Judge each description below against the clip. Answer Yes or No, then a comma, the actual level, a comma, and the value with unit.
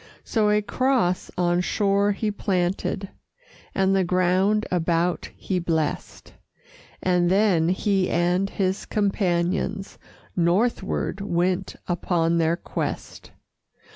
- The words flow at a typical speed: No, slow, 105 wpm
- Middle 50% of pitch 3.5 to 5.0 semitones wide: No, narrow, 2.4 semitones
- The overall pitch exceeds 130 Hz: Yes, medium, 185 Hz